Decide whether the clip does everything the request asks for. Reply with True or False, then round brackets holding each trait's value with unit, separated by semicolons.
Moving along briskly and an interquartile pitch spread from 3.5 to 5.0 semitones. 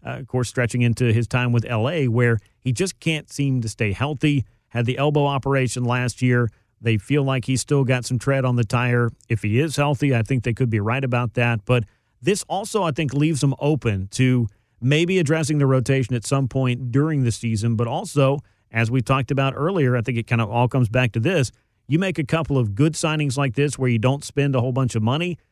False (235 wpm; 3.1 semitones)